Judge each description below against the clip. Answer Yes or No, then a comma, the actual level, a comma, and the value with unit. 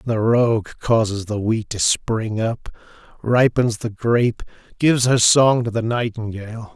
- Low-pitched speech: Yes, low, 115 Hz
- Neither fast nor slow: Yes, average, 150 wpm